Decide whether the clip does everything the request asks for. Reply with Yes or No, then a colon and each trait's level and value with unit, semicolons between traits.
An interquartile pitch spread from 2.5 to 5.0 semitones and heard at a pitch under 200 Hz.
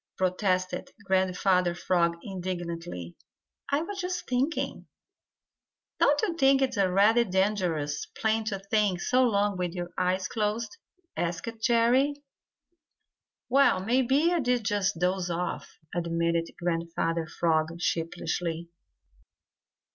No: wide, 5.5 semitones; high, 190 Hz